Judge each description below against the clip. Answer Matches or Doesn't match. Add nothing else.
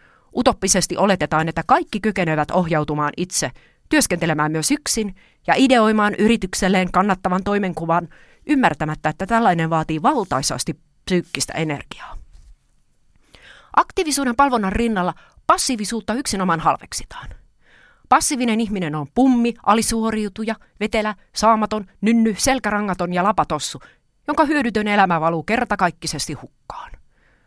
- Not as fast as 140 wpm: Matches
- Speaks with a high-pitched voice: Matches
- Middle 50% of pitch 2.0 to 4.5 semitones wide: Doesn't match